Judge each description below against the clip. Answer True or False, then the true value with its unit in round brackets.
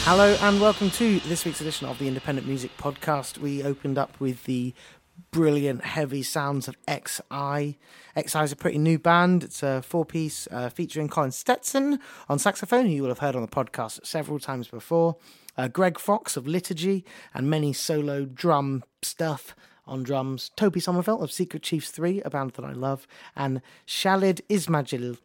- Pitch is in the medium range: True (150 Hz)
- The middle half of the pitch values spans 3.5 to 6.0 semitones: True (4.6 semitones)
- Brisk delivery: False (175 wpm)